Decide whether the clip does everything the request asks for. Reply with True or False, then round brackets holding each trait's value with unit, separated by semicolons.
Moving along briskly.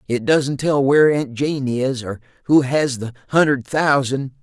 False (175 wpm)